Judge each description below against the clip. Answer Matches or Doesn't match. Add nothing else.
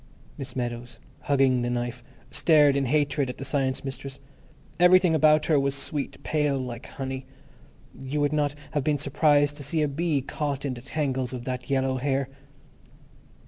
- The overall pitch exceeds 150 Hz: Doesn't match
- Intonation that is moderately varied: Doesn't match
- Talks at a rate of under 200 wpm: Matches